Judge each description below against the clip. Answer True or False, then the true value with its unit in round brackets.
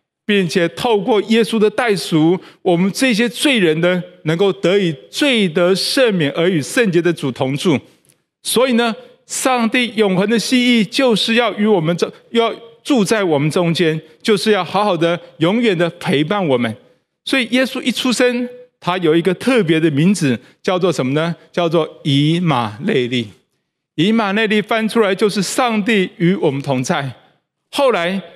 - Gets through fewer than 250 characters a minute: True (240 characters per minute)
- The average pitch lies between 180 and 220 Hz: True (190 Hz)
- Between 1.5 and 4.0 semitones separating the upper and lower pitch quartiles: False (5.5 semitones)